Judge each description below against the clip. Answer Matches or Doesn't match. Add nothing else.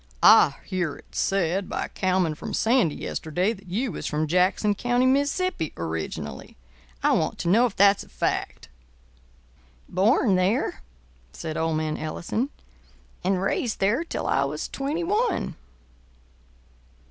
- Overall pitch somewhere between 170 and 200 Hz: Matches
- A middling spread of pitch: Doesn't match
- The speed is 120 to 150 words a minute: Matches